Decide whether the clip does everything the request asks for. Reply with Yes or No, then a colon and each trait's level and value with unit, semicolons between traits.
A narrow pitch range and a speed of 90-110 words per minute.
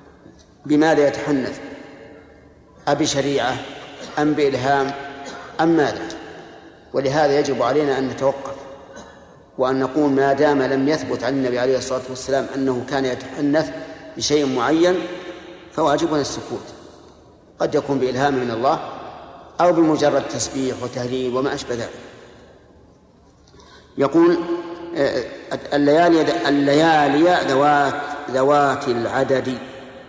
Yes: narrow, 2.2 semitones; average, 95 wpm